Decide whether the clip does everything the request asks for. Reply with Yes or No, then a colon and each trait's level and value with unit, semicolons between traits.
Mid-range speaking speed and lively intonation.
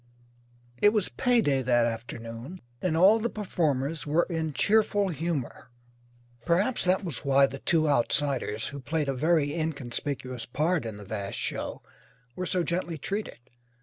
Yes: average, 150 wpm; wide, 5.8 semitones